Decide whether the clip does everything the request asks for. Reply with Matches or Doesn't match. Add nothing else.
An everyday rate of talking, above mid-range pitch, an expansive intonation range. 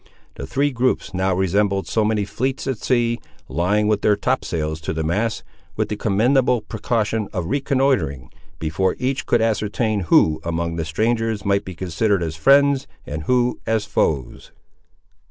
Doesn't match